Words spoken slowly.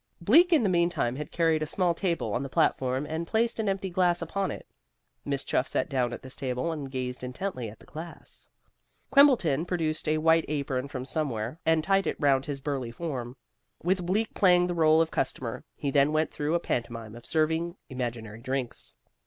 No: average, 195 wpm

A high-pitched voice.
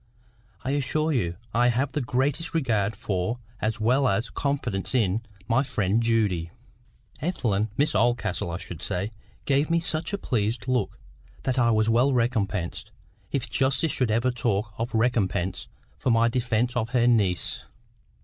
No: low, 115 Hz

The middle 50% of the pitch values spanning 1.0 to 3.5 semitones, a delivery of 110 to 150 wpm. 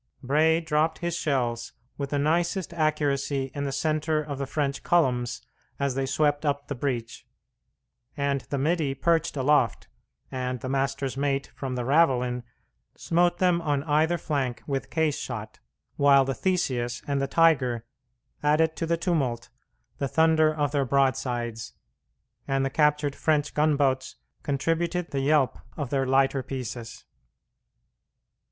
Yes: average, 2.8 semitones; average, 145 wpm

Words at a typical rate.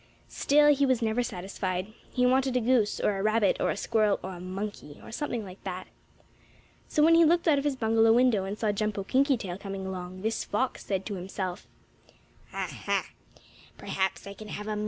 Yes: average, 175 wpm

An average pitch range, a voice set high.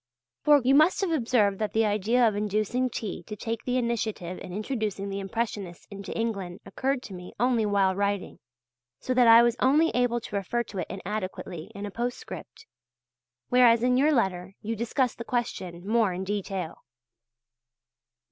Yes: average, 3.8 semitones; high, 220 Hz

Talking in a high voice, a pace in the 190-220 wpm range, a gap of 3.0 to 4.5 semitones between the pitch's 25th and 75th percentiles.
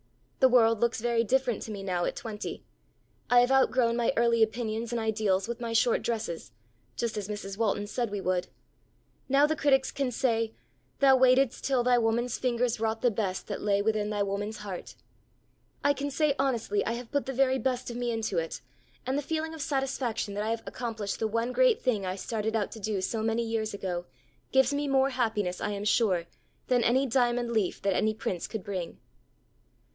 Yes: high, 230 Hz; average, 200 wpm; average, 3.3 semitones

